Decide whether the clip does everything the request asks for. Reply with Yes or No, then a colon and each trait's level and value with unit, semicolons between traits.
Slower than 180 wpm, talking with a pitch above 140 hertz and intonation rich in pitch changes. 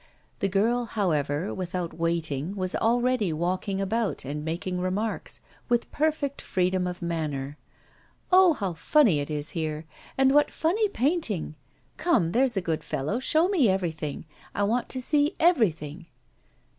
Yes: average, 145 wpm; high, 190 Hz; wide, 7.4 semitones